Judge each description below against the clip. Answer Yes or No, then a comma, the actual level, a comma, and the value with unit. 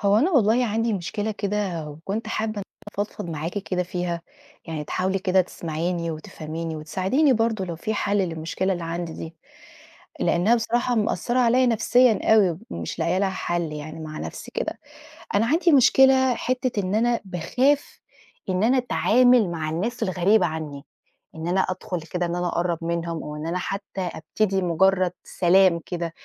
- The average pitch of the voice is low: No, medium, 185 Hz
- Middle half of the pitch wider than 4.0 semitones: Yes, average, 4.7 semitones